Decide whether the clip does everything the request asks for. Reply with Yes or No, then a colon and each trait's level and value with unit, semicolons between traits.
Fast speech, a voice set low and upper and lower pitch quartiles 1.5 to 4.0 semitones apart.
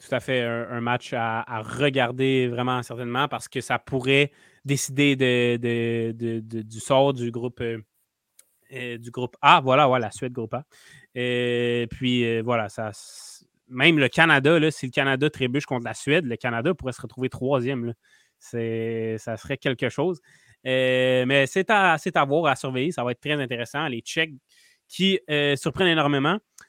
No: average, 185 wpm; low, 130 Hz; average, 3.0 semitones